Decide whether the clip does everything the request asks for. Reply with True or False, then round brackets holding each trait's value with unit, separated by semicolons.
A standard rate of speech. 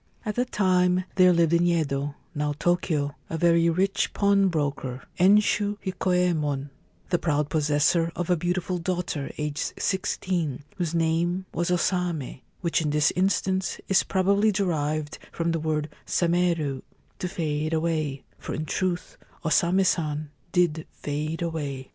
True (150 wpm)